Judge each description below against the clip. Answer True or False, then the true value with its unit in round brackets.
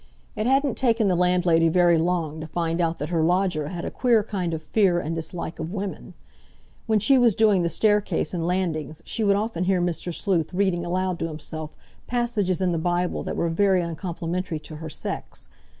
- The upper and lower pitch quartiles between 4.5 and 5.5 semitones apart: False (3.2 semitones)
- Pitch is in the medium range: True (180 Hz)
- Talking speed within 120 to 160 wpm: False (195 wpm)